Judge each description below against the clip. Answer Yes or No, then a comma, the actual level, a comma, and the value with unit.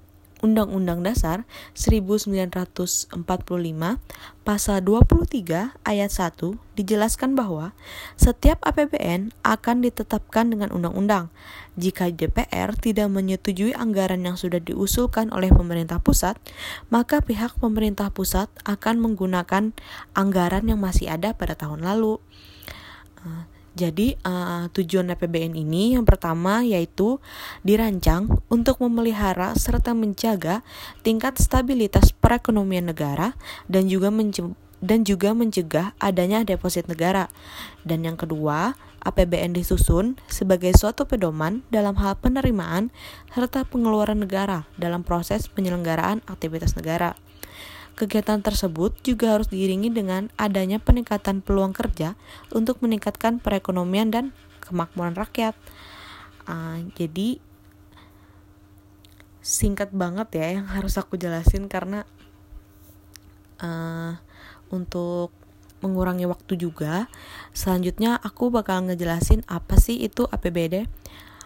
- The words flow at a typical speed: Yes, average, 105 wpm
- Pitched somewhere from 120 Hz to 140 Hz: No, high, 190 Hz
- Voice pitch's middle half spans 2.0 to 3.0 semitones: No, average, 4.3 semitones